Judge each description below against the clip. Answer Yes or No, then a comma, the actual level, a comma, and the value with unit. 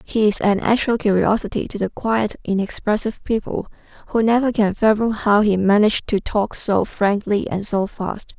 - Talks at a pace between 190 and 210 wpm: No, average, 170 wpm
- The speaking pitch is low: No, high, 210 Hz